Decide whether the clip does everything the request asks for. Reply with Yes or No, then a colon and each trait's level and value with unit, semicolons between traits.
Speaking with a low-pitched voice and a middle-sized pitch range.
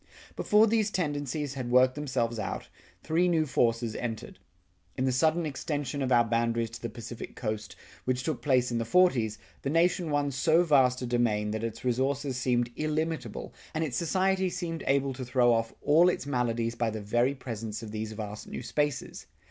Yes: low, 130 Hz; average, 4.6 semitones